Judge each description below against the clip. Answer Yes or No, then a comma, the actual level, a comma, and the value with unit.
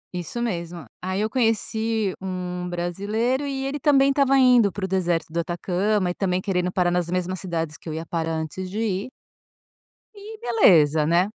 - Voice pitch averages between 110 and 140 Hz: No, medium, 185 Hz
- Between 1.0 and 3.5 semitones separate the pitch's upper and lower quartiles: No, average, 4.4 semitones